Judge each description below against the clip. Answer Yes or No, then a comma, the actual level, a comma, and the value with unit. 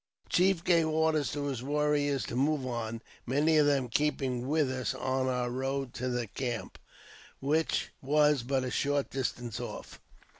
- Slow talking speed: No, average, 165 wpm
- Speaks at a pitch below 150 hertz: Yes, low, 135 Hz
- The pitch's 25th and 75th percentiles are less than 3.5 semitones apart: Yes, average, 2.8 semitones